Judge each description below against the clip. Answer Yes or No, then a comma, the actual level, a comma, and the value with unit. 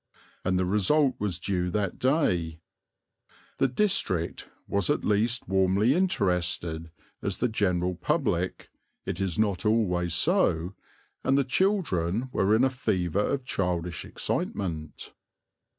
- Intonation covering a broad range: Yes, wide, 5.9 semitones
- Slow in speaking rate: Yes, slow, 125 wpm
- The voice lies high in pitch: No, very low, 95 Hz